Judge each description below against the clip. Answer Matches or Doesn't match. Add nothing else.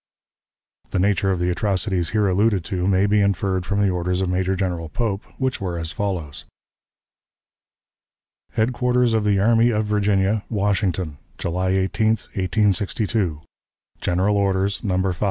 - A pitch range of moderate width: Doesn't match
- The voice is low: Matches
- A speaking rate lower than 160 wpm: Matches